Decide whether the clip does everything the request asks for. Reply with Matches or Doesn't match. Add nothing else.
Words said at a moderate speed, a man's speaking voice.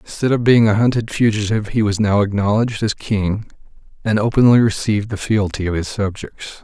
Matches